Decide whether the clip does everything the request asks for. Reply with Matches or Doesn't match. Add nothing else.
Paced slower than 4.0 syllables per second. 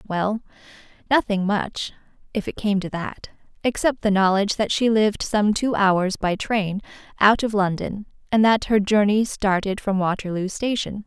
Doesn't match